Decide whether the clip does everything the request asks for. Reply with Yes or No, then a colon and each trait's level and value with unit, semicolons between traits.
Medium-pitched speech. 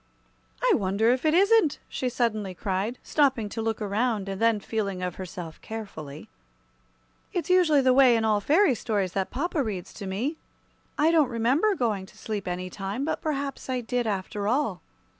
No: high, 225 Hz